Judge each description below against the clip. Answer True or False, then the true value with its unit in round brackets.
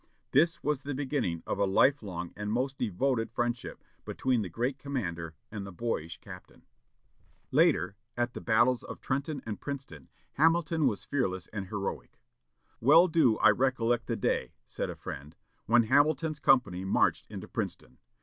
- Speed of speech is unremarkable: True (160 wpm)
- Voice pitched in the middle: False (120 Hz)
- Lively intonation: True (6.0 semitones)